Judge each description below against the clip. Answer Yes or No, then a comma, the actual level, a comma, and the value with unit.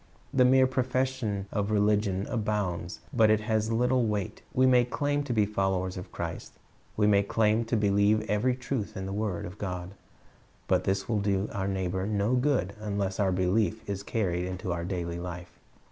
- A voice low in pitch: Yes, low, 105 Hz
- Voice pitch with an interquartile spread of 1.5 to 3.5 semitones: Yes, average, 3.0 semitones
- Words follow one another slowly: No, average, 180 wpm